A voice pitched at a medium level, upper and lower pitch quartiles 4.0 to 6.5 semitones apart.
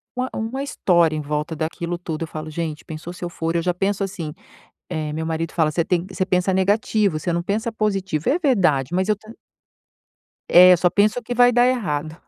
Yes: medium, 180 Hz; average, 4.5 semitones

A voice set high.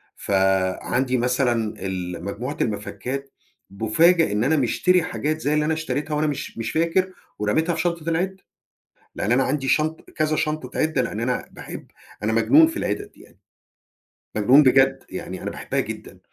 No: low, 135 Hz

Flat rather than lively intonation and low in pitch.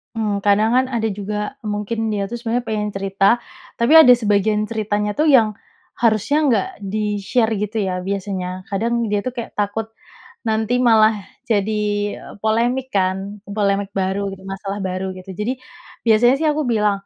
No: narrow, 2.2 semitones; high, 210 Hz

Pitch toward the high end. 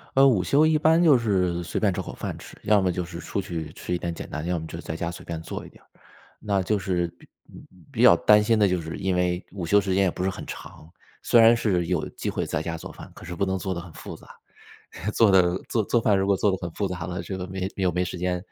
No: very low, 90 Hz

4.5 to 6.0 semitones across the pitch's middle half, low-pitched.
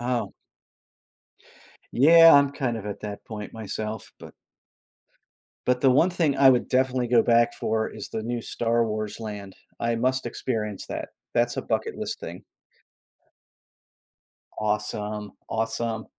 No: average, 2.9 semitones; low, 115 Hz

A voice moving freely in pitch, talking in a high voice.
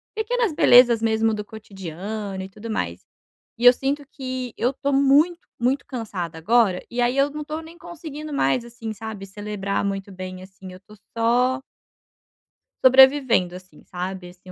Yes: wide, 5.8 semitones; high, 225 Hz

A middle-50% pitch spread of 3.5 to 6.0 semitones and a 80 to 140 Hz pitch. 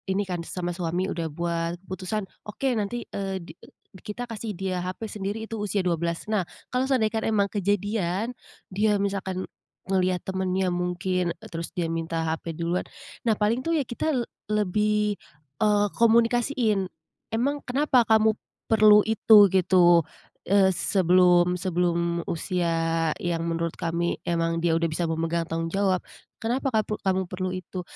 No: average, 3.8 semitones; high, 190 Hz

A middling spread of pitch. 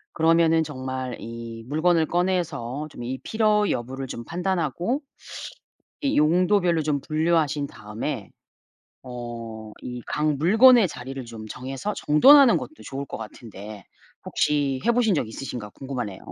No: wide, 6.2 semitones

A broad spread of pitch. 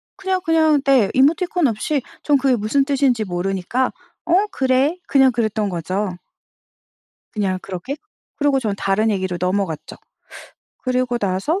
Yes: wide, 6.3 semitones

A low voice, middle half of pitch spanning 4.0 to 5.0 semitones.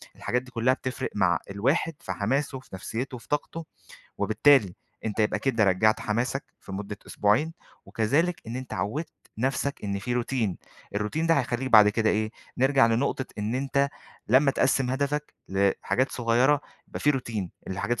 Yes: low, 125 Hz; average, 4.3 semitones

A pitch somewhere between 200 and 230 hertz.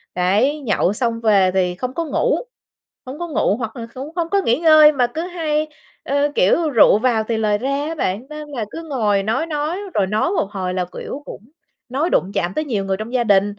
No: very high, 250 Hz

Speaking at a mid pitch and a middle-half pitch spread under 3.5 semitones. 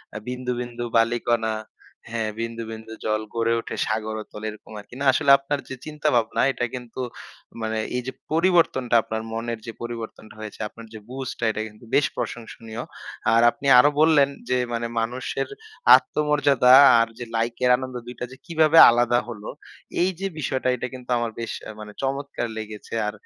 No: low, 120 Hz; average, 2.8 semitones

